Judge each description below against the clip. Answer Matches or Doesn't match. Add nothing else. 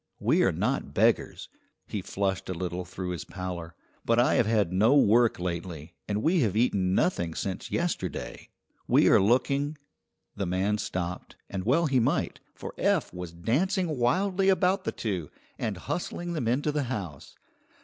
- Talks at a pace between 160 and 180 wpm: Matches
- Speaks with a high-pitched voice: Doesn't match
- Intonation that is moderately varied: Doesn't match